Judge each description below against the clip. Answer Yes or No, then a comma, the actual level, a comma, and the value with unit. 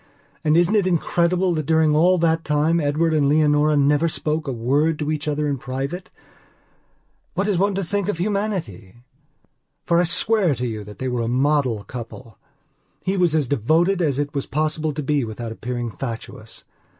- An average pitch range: Yes, average, 4.2 semitones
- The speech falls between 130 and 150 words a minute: No, average, 185 wpm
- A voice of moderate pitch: Yes, medium, 150 Hz